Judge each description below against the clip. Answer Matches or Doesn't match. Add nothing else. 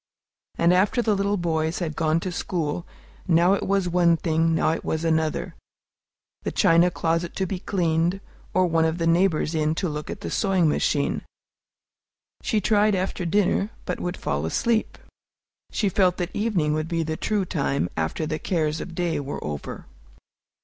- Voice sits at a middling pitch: Matches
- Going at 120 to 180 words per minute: Matches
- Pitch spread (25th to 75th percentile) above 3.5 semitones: Doesn't match